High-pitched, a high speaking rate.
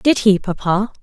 No: high, 205 Hz; average, 175 wpm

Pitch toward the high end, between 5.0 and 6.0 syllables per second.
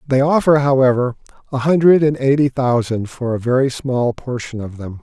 No: low, 130 Hz; 5.1 syllables/s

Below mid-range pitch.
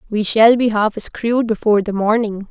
No: high, 215 Hz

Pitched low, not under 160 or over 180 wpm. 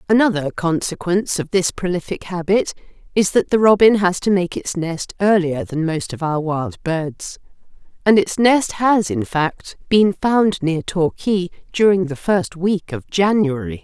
No: medium, 180 Hz; average, 165 wpm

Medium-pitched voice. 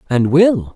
Yes: medium, 150 Hz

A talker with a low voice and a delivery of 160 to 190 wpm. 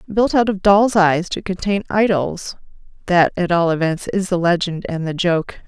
No: medium, 185 Hz; average, 180 wpm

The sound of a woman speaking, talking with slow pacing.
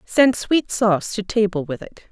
No: female; average, 200 wpm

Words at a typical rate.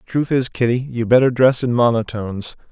Yes: average, 175 wpm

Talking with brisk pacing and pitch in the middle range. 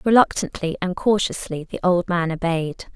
No: average, 140 wpm; medium, 180 Hz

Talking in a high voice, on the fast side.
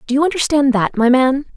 Yes: very high, 270 Hz; fast, 230 wpm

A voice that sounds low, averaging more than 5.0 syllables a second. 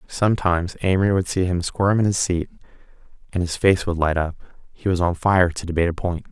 Yes: very low, 90 Hz; 6.1 syllables/s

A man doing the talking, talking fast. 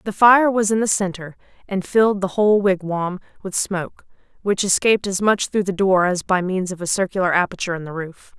No: female; fast, 215 wpm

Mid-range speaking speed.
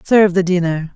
Yes: average, 190 wpm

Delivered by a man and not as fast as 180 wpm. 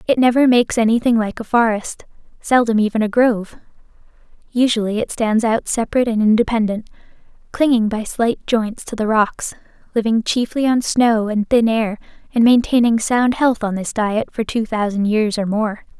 No: female; average, 170 wpm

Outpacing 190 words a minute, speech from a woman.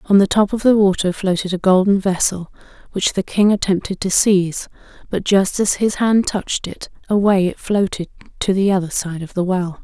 Yes: average, 200 wpm; female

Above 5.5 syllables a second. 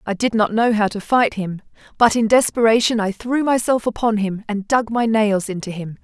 No: 5.1 syllables/s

